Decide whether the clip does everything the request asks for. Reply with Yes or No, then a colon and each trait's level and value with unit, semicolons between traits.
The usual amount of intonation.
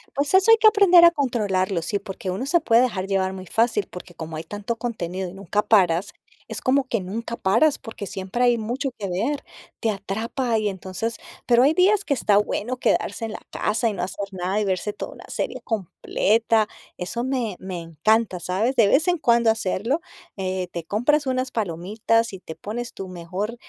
Yes: average, 4.5 semitones